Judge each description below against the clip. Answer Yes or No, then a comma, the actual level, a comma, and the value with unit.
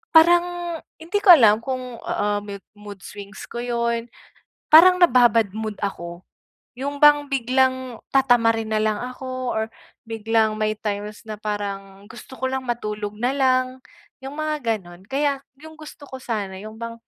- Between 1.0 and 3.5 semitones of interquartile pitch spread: No, average, 4.1 semitones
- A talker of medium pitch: No, high, 235 Hz